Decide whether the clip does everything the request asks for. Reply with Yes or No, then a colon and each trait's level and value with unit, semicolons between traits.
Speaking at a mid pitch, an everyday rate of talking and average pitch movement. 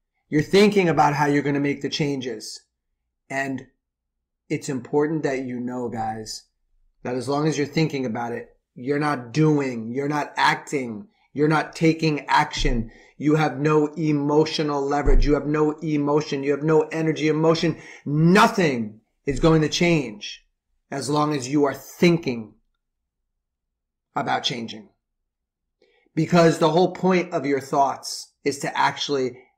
Yes: medium, 145 Hz; average, 145 wpm; average, 3.7 semitones